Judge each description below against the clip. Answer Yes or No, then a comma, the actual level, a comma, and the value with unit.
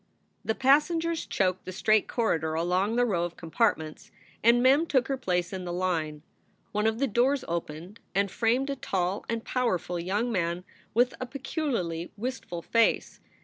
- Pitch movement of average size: No, wide, 6.1 semitones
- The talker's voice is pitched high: Yes, high, 210 Hz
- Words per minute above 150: Yes, average, 165 wpm